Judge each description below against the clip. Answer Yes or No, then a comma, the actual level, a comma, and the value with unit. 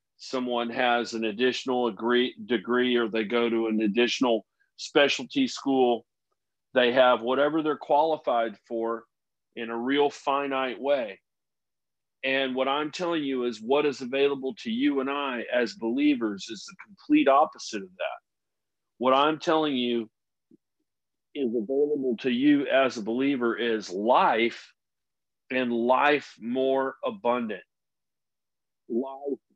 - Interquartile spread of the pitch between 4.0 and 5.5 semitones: No, average, 3.2 semitones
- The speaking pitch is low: Yes, low, 130 Hz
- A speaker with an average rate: No, slow, 130 wpm